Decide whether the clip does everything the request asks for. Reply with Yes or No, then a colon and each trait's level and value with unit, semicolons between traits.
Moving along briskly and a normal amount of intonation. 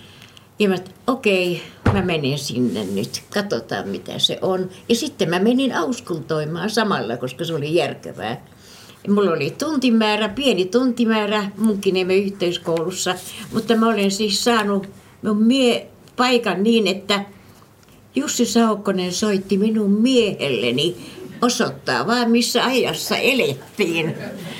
No: average, 125 wpm; average, 4.0 semitones